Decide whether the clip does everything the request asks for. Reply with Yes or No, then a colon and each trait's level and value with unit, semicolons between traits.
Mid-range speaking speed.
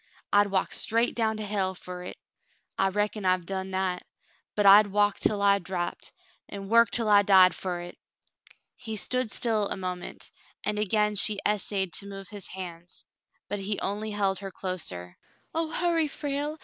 Yes: average, 185 wpm